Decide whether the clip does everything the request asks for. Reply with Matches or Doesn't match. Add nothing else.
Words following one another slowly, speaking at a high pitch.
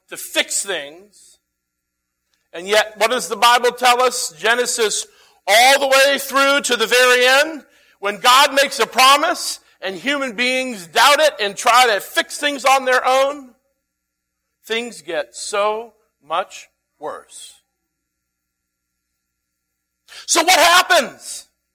Matches